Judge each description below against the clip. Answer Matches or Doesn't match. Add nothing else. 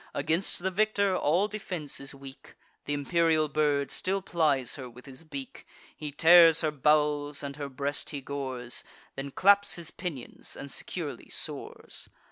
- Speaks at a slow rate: Doesn't match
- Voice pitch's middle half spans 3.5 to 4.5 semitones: Matches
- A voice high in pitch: Doesn't match